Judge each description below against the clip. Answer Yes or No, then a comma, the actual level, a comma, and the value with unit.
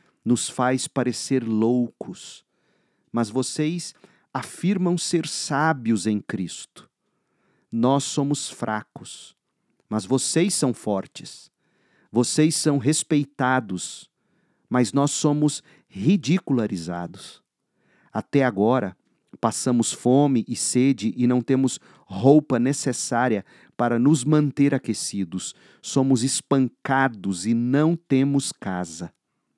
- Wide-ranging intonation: No, average, 3.9 semitones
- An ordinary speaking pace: No, slow, 95 wpm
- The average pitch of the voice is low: Yes, low, 130 Hz